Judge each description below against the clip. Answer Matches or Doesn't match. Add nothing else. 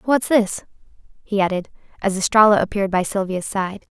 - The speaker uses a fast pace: Doesn't match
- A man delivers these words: Doesn't match